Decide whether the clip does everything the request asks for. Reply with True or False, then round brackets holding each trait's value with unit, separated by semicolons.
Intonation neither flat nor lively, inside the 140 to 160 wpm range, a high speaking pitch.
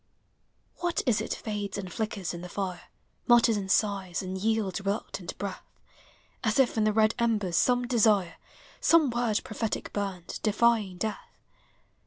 True (3.1 semitones; 150 wpm; 210 Hz)